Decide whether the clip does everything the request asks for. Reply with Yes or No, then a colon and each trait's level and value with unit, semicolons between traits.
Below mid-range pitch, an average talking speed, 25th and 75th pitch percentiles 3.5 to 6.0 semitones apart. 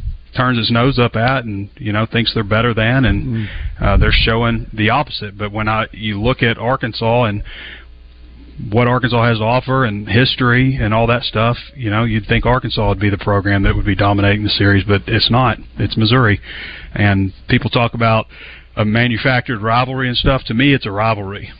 No: low, 115 Hz; average, 195 wpm; average, 2.8 semitones